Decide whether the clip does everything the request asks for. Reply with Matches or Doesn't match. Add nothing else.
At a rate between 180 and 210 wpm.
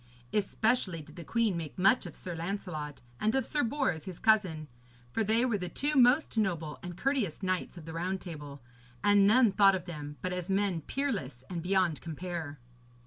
Matches